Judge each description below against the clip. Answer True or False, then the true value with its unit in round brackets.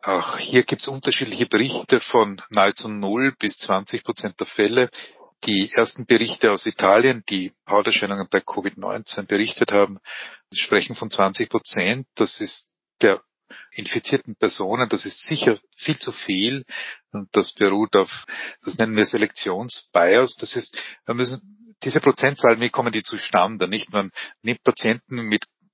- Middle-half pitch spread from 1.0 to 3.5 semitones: False (4.3 semitones)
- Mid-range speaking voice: False (115 Hz)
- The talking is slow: False (145 wpm)